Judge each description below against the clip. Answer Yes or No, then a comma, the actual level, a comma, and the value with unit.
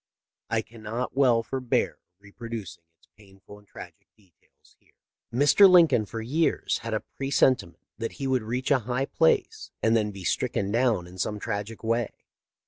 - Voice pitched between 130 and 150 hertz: No, low, 115 Hz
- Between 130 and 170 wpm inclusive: Yes, average, 165 wpm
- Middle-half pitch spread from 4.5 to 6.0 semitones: No, average, 3.8 semitones